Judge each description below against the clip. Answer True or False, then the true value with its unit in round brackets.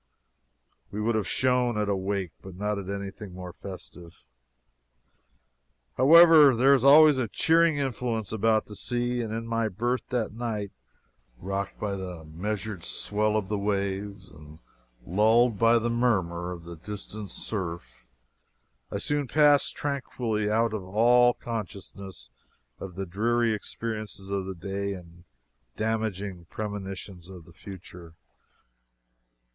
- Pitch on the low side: True (105 Hz)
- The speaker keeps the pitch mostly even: False (3.6 semitones)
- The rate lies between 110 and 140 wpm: True (135 wpm)